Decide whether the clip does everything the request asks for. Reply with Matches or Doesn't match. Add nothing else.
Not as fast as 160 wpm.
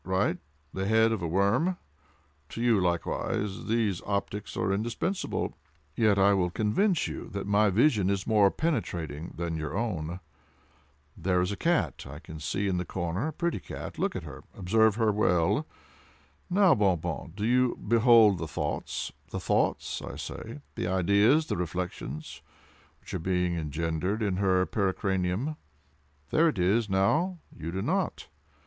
Matches